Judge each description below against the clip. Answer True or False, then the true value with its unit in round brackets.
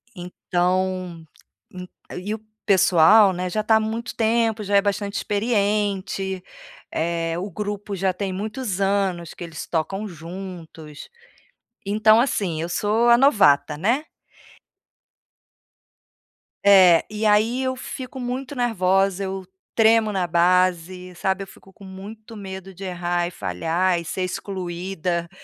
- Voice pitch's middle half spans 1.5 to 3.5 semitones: True (3.1 semitones)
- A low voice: False (195 Hz)